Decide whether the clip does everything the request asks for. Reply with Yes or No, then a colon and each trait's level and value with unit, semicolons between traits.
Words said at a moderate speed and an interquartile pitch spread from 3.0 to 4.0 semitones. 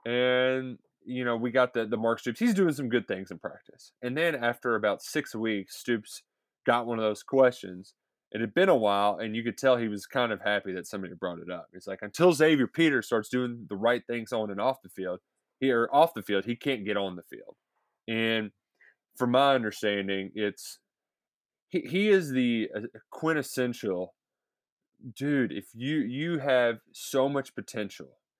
Yes: average, 190 wpm; average, 3.7 semitones